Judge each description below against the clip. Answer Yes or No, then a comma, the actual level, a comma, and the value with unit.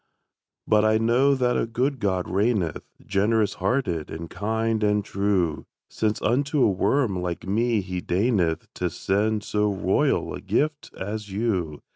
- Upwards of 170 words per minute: No, average, 150 wpm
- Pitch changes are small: No, average, 3.7 semitones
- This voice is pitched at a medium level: No, low, 105 Hz